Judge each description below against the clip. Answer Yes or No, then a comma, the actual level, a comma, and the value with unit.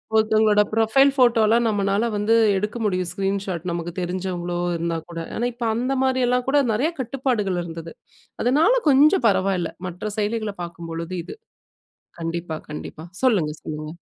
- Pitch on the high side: Yes, high, 205 Hz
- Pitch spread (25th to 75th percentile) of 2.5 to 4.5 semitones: No, wide, 5.5 semitones